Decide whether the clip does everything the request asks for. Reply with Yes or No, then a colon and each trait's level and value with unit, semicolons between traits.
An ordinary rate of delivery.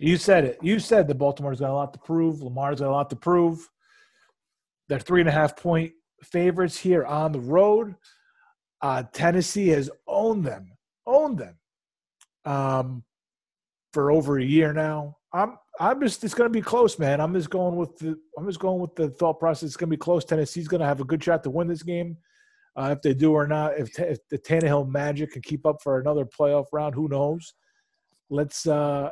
No: fast, 210 wpm